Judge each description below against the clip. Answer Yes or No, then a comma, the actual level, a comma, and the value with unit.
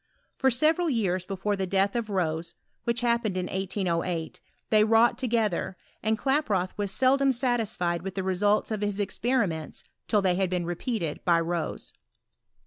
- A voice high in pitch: Yes, high, 200 Hz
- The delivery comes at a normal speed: Yes, average, 165 wpm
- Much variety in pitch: No, average, 4.5 semitones